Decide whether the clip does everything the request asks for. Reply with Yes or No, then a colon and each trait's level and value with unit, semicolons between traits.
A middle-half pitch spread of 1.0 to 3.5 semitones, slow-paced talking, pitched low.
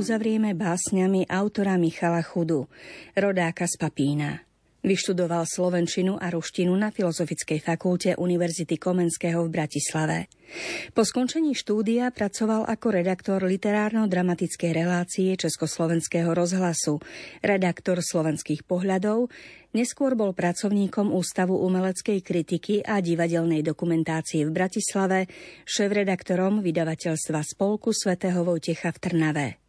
No: average, 2.9 semitones; slow, 100 wpm; medium, 180 Hz